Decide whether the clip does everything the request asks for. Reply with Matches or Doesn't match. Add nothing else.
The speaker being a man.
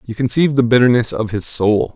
Matches